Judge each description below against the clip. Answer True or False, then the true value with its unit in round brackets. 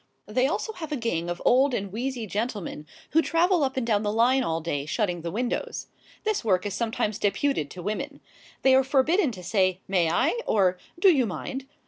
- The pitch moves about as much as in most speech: False (6.3 semitones)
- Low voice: False (225 Hz)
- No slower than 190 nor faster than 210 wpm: True (200 wpm)